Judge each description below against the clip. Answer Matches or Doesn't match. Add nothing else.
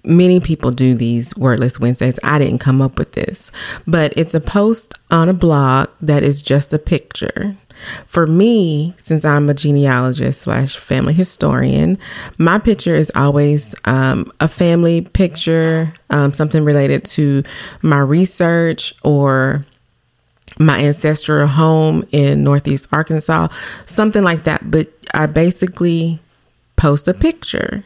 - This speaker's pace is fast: Doesn't match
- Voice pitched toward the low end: Doesn't match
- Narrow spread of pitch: Doesn't match